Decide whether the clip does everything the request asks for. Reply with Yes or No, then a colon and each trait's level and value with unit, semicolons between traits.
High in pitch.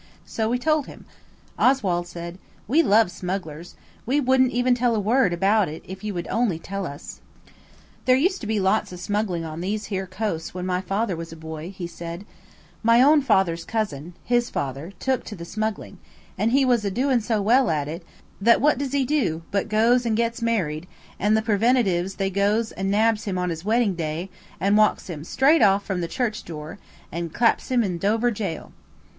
Yes: high, 205 Hz